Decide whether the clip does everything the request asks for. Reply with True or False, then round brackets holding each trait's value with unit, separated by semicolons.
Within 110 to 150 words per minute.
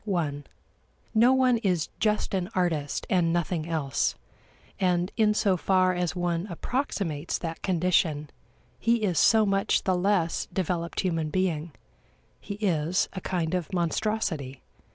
True (135 wpm)